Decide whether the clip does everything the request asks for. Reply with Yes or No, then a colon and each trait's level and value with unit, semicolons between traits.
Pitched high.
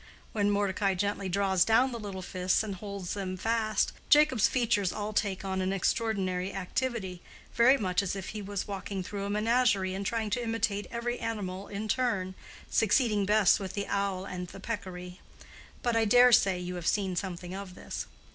Yes: high, 200 Hz